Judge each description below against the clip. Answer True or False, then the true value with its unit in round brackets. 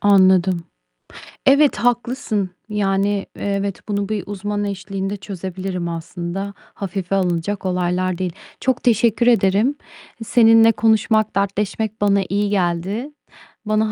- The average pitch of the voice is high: True (200 Hz)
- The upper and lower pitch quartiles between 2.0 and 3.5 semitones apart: True (2.5 semitones)